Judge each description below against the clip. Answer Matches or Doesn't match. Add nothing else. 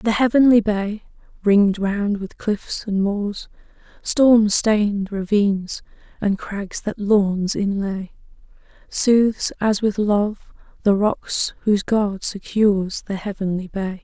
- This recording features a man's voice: Doesn't match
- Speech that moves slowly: Matches